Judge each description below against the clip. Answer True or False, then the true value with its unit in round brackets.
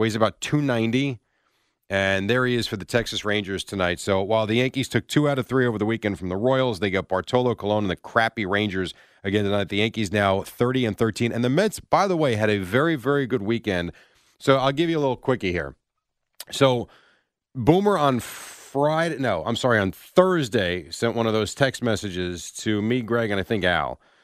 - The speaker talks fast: True (215 wpm)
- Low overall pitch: True (115 Hz)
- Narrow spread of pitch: False (4.4 semitones)